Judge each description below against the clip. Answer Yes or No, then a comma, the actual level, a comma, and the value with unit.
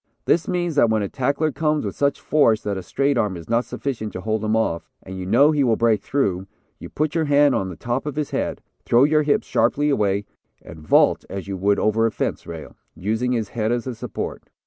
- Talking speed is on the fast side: Yes, fast, 235 wpm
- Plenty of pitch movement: Yes, wide, 5.9 semitones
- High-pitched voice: No, low, 115 Hz